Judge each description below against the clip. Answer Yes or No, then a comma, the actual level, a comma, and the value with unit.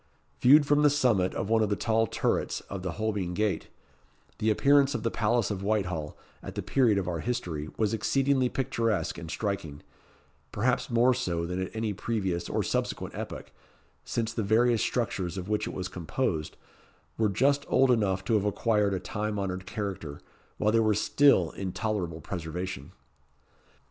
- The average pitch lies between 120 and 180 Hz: No, low, 105 Hz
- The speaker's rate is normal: Yes, average, 175 wpm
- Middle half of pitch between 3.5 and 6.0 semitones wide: Yes, average, 4.0 semitones